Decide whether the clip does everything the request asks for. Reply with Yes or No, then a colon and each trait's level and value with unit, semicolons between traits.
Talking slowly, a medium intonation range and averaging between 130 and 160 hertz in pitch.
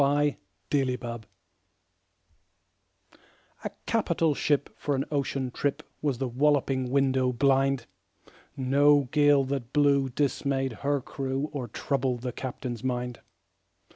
No: slow, 125 wpm; narrow, 2.0 semitones; low, 135 Hz